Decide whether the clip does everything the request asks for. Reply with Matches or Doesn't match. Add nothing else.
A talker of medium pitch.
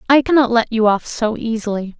Doesn't match